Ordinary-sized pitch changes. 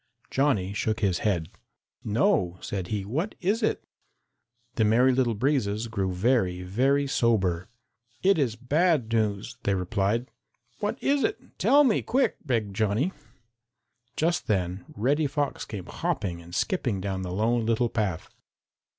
No: wide, 6.1 semitones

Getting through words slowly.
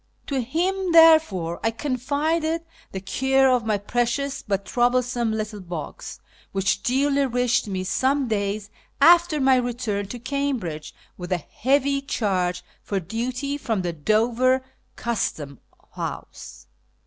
Yes: slow, 125 wpm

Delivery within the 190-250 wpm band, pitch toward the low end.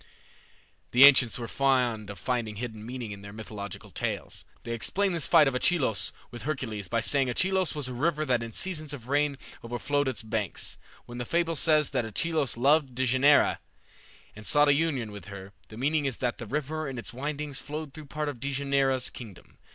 Yes: average, 200 wpm; low, 130 Hz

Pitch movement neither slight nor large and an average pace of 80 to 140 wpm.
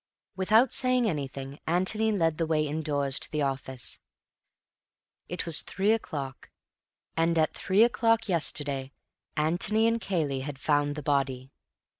No: wide, 6.0 semitones; slow, 135 wpm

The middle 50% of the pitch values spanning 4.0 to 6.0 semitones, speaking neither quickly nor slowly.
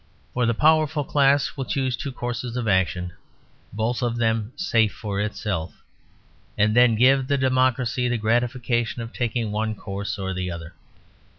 No: average, 3.4 semitones; average, 160 wpm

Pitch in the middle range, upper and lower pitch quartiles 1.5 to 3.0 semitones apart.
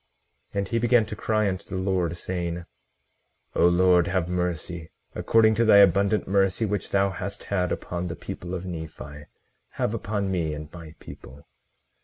No: very low, 95 Hz; narrow, 2.6 semitones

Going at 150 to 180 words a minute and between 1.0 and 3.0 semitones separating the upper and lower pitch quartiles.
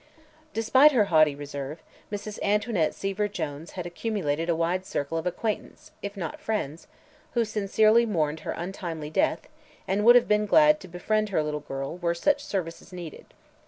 No: average, 165 wpm; average, 5.0 semitones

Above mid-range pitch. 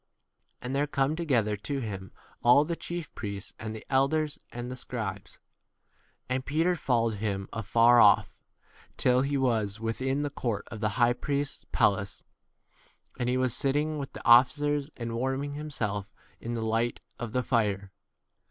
No: low, 125 Hz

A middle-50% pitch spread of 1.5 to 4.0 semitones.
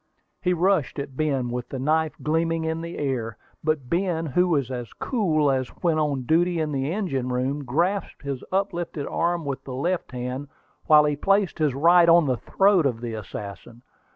No: average, 4.6 semitones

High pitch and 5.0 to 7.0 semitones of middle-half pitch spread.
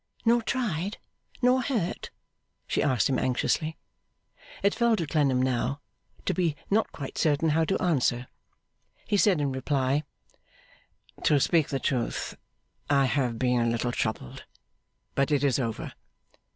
No: medium, 145 Hz; average, 5.3 semitones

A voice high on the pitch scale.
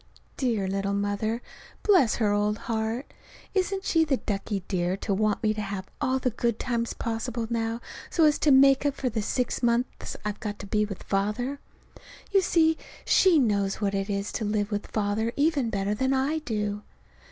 Yes: high, 225 Hz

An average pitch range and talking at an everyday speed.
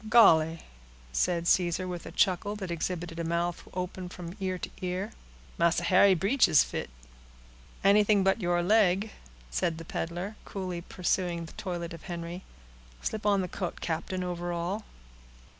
No: narrow, 2.1 semitones; average, 150 wpm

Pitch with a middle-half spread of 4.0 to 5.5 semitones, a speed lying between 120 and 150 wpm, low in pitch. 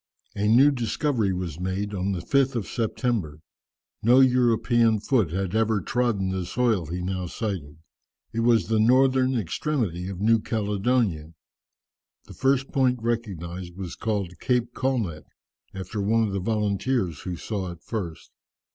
Yes: average, 4.7 semitones; average, 145 wpm; low, 105 Hz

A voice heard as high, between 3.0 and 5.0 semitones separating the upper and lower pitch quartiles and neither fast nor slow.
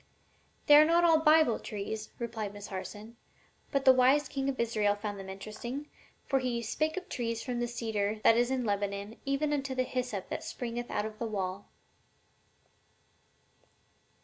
Yes: high, 235 Hz; average, 4.4 semitones; average, 175 wpm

